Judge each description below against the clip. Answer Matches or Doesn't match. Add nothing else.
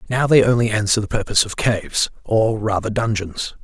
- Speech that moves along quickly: Doesn't match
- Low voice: Matches